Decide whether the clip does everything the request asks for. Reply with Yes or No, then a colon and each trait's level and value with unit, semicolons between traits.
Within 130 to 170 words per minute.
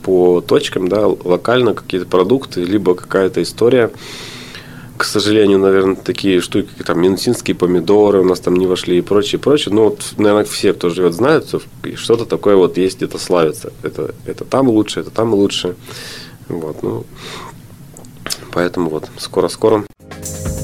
Yes: average, 150 wpm